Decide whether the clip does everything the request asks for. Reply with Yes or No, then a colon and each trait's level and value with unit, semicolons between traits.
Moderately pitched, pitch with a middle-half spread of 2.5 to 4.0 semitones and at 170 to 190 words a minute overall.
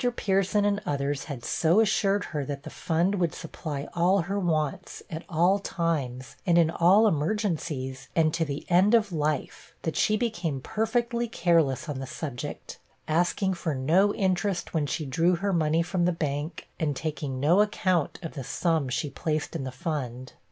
No: medium, 165 Hz; average, 4.6 semitones; average, 175 wpm